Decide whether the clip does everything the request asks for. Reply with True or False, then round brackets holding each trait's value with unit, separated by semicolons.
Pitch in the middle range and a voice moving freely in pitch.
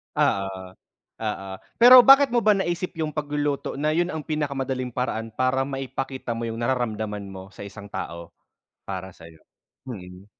False (130 Hz; 6.7 semitones)